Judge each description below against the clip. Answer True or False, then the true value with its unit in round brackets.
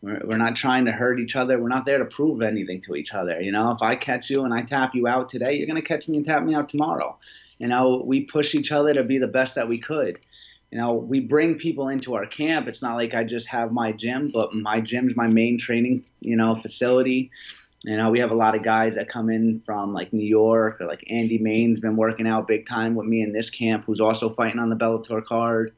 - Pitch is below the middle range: True (115 Hz)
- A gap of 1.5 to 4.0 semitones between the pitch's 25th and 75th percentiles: True (2.5 semitones)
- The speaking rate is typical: False (260 wpm)